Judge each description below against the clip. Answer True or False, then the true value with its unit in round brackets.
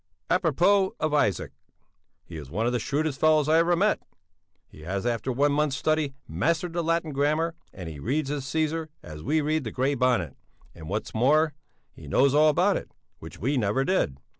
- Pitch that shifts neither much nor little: False (5.9 semitones)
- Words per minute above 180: True (195 wpm)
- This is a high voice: False (145 Hz)